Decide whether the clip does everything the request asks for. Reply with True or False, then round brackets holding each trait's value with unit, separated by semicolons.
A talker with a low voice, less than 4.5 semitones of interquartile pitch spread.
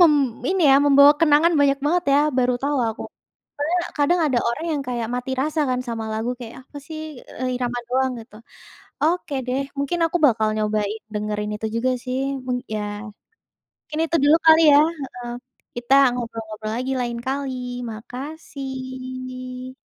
False (255 Hz; 3.4 semitones)